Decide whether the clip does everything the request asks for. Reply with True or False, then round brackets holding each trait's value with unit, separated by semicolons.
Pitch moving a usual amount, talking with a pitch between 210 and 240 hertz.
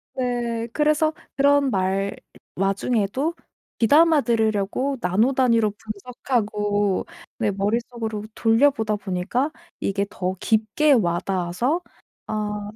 True (4.3 semitones; 220 Hz)